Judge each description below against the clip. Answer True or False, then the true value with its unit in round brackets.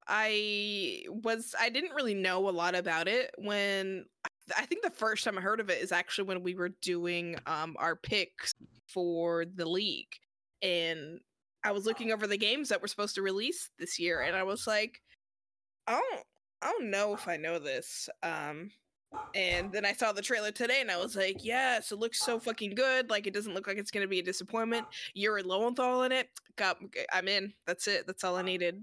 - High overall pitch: True (200 Hz)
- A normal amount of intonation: True (3.7 semitones)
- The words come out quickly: True (210 wpm)